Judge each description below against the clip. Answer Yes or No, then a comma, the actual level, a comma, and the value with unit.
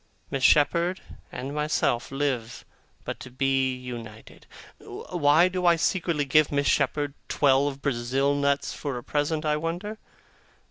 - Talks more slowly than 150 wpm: Yes, slow, 135 wpm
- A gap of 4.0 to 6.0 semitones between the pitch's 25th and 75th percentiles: No, average, 2.7 semitones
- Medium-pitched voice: Yes, medium, 145 Hz